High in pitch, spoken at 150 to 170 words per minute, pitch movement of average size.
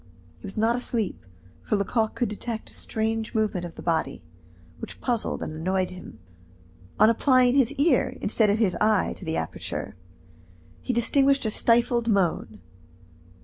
Yes: high, 220 Hz; average, 155 wpm; average, 4.0 semitones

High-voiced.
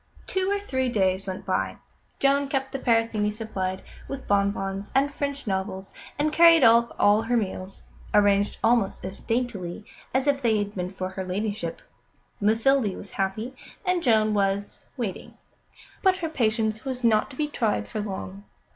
Yes: high, 220 Hz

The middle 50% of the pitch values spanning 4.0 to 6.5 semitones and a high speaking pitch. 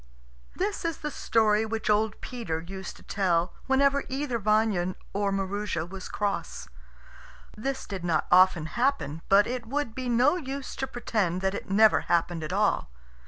Yes: average, 5.3 semitones; high, 210 Hz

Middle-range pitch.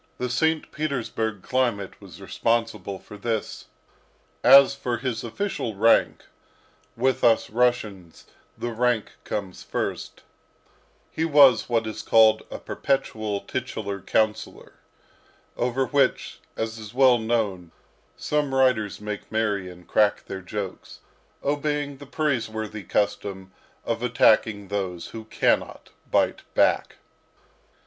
No: low, 115 Hz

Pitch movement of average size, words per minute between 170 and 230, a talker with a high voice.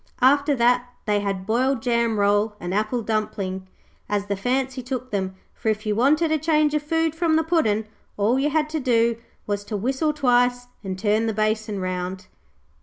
Yes: average, 4.8 semitones; average, 185 wpm; high, 235 Hz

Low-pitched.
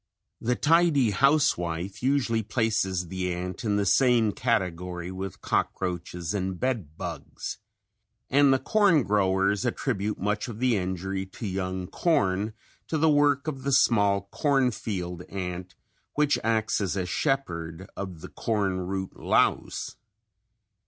Yes: low, 100 Hz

